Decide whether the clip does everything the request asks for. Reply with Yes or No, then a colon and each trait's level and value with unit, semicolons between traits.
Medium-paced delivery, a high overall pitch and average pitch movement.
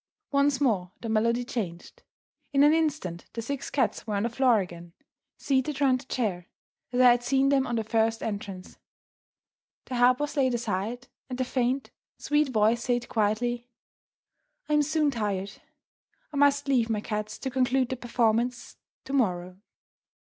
Yes: average, 165 wpm; high, 245 Hz; average, 3.8 semitones